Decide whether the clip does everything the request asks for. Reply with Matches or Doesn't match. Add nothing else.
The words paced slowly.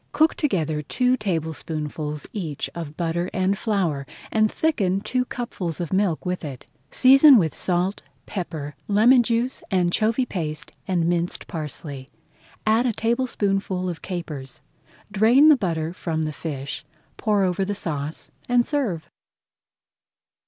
Matches